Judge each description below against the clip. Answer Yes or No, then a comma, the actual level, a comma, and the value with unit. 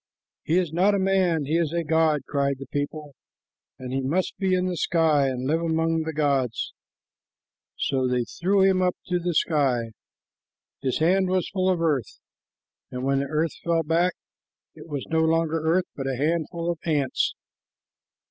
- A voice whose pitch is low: No, medium, 160 Hz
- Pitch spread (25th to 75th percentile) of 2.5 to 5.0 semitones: Yes, average, 3.8 semitones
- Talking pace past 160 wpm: Yes, average, 175 wpm